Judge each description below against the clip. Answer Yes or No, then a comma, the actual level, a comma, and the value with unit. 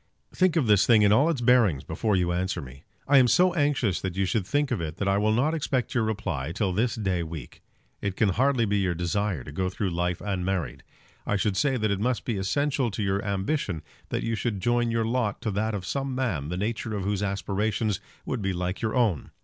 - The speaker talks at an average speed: No, fast, 240 wpm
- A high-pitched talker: No, low, 105 Hz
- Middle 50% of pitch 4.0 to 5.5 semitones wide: Yes, average, 4.4 semitones